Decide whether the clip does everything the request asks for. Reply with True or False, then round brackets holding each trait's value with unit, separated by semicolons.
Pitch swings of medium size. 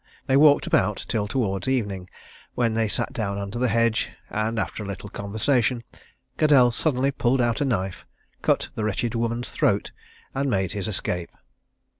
True (3.8 semitones)